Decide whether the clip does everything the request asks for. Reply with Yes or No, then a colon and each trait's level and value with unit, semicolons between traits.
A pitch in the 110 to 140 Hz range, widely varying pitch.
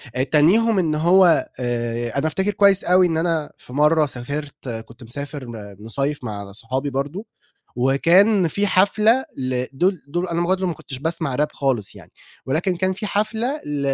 No: medium, 150 Hz; wide, 6.2 semitones